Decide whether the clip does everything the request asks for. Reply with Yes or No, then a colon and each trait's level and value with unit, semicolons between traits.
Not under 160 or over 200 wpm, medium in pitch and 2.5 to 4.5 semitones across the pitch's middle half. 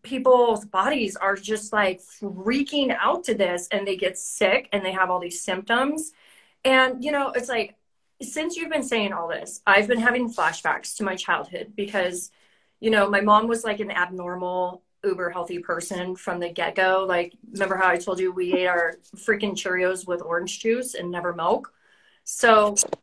No: average, 185 wpm; high, 200 Hz; average, 4.0 semitones